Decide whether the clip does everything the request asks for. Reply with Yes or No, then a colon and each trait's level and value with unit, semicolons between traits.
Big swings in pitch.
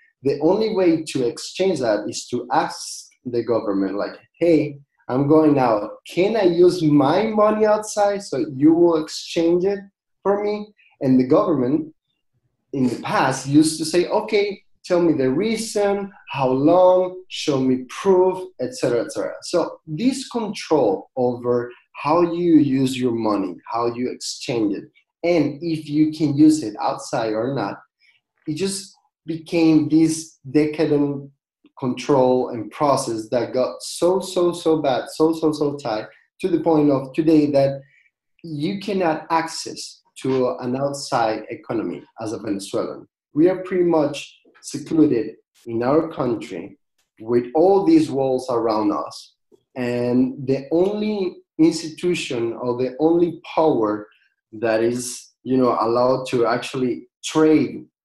Yes: wide, 5.8 semitones